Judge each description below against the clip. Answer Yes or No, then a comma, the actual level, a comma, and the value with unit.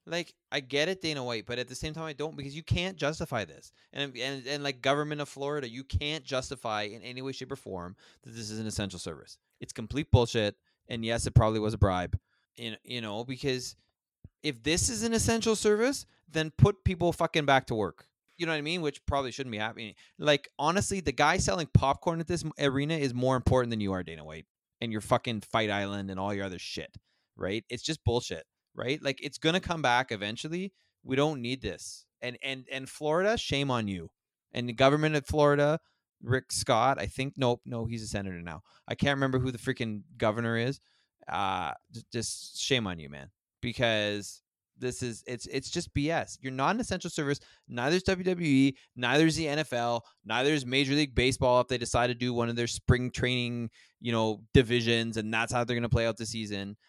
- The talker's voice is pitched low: Yes, low, 125 Hz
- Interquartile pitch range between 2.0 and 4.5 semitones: Yes, average, 4.2 semitones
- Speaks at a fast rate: Yes, fast, 210 wpm